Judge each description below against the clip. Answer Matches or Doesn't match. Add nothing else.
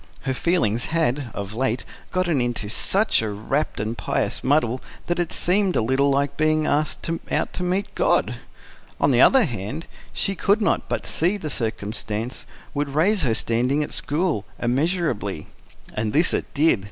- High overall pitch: Doesn't match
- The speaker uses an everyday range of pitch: Doesn't match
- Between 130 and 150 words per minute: Doesn't match